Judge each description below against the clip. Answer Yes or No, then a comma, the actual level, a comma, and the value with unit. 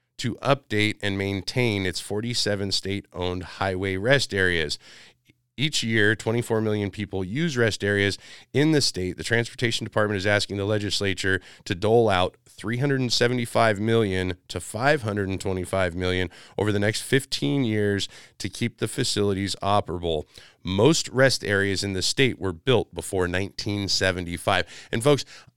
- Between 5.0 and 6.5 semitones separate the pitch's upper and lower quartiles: No, average, 3.7 semitones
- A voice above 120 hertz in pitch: No, low, 105 Hz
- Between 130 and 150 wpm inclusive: Yes, slow, 135 wpm